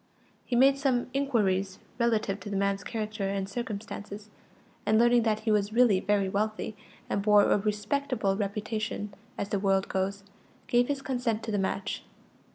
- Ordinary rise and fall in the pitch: Yes, average, 3.0 semitones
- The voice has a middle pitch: No, high, 210 Hz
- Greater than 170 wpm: No, average, 165 wpm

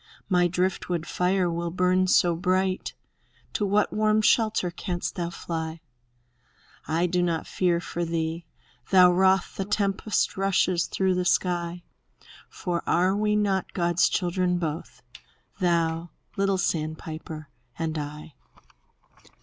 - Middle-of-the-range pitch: Yes, medium, 180 Hz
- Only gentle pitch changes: Yes, narrow, 2.1 semitones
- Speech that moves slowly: Yes, slow, 125 wpm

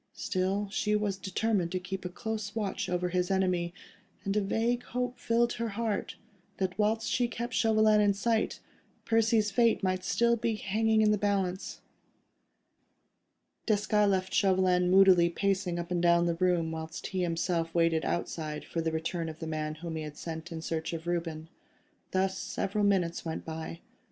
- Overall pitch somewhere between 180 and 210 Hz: Yes, high, 190 Hz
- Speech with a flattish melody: No, average, 3.7 semitones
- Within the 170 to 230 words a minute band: Yes, average, 175 wpm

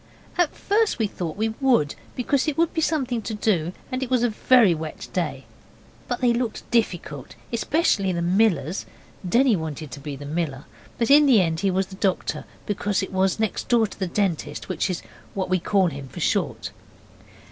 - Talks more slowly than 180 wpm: No, average, 190 wpm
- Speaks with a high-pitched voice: Yes, high, 200 Hz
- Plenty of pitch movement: Yes, wide, 6.2 semitones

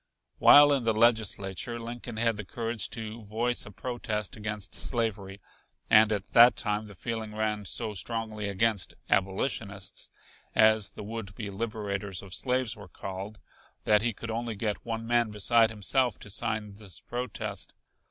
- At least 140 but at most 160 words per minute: Yes, average, 155 wpm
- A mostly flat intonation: Yes, narrow, 2.3 semitones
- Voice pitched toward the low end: Yes, low, 110 Hz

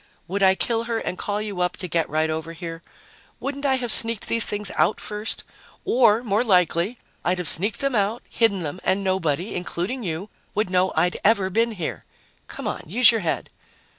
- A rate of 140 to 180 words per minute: No, average, 195 wpm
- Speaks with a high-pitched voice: Yes, high, 200 Hz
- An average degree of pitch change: Yes, average, 4.2 semitones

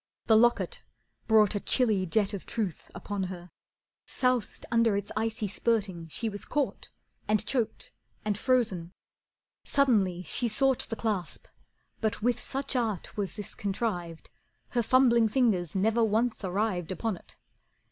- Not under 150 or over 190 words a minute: No, average, 140 wpm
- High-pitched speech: Yes, high, 215 Hz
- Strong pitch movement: No, average, 3.6 semitones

